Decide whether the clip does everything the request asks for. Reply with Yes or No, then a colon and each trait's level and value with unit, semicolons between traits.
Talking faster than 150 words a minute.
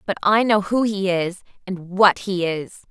Yes: fast, 205 wpm